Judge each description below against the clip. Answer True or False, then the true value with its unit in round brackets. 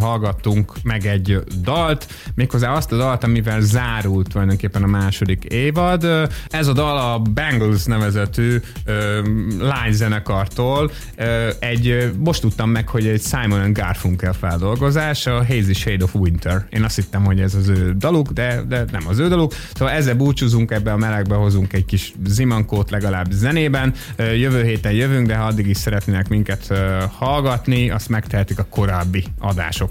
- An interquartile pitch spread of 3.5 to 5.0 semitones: True (3.8 semitones)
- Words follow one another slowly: False (155 wpm)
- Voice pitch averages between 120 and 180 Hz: False (110 Hz)